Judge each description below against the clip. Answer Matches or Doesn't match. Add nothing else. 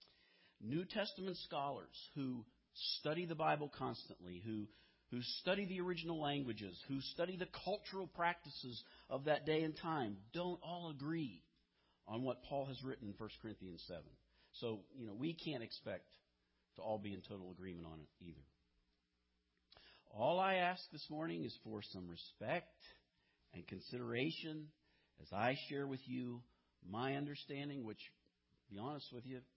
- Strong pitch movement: Matches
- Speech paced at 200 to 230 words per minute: Doesn't match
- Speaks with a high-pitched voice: Doesn't match